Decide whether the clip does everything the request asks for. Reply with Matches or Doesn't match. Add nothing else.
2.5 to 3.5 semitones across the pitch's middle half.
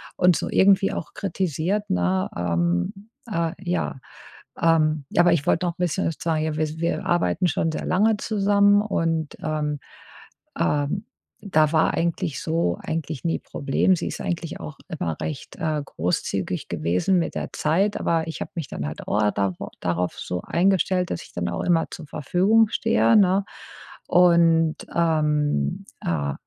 Doesn't match